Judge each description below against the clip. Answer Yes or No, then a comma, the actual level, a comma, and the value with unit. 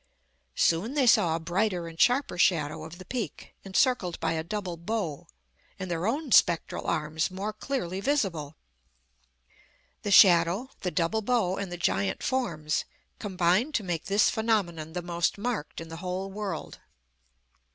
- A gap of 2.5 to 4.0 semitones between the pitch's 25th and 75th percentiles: No, average, 4.4 semitones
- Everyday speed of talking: Yes, average, 150 wpm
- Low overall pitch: No, medium, 185 Hz